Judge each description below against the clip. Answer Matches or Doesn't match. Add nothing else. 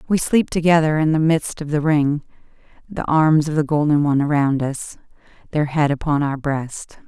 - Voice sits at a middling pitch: Matches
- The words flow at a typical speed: Matches